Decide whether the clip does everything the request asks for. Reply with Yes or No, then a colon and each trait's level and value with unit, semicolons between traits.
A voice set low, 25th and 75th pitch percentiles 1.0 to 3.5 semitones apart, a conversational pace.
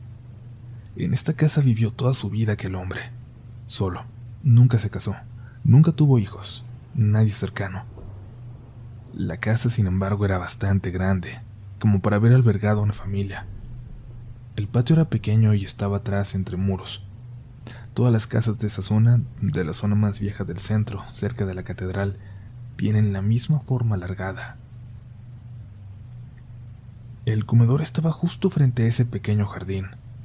Yes: low, 115 Hz; average, 3.1 semitones; average, 145 wpm